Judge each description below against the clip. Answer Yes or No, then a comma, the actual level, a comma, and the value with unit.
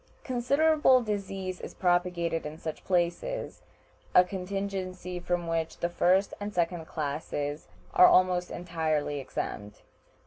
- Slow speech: Yes, slow, 115 wpm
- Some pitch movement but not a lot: Yes, average, 3.0 semitones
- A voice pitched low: No, medium, 180 Hz